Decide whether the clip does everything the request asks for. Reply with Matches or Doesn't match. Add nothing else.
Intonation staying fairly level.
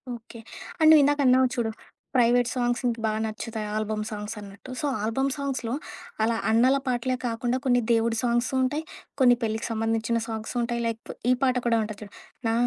Matches